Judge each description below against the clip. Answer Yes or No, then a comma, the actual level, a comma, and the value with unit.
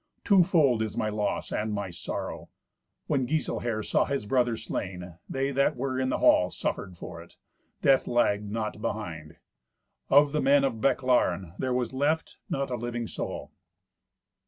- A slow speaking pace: No, average, 160 wpm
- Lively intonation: No, average, 4.7 semitones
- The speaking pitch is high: No, low, 120 Hz